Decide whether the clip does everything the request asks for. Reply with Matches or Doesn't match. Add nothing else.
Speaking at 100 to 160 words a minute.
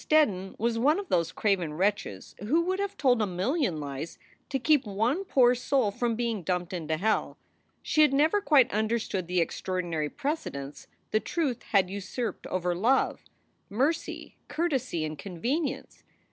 Matches